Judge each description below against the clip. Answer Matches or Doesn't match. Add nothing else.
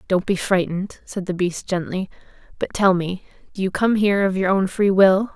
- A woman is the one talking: Matches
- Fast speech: Matches